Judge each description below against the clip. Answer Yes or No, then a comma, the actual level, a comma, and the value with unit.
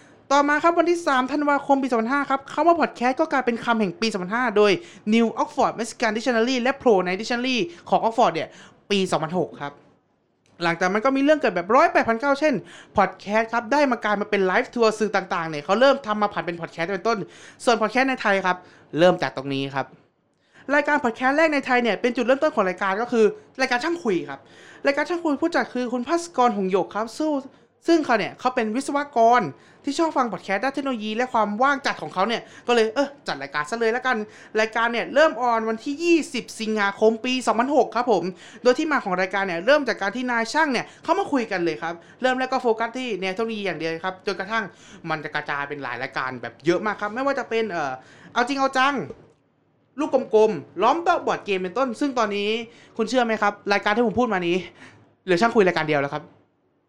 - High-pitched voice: Yes, high, 230 Hz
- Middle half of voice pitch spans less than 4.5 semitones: No, average, 5.3 semitones